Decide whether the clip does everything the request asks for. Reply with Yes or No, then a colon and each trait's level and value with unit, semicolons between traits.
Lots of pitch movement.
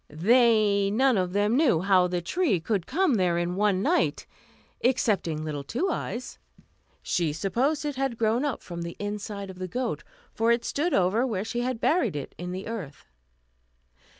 Yes: wide, 5.7 semitones